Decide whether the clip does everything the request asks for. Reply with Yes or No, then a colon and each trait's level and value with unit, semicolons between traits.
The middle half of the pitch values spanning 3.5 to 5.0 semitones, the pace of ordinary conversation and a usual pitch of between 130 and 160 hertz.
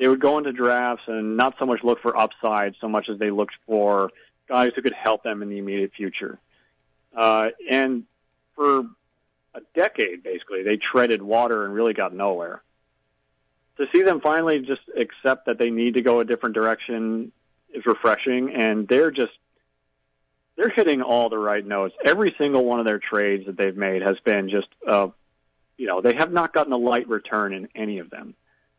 No: average, 3.9 semitones; average, 190 wpm; low, 110 Hz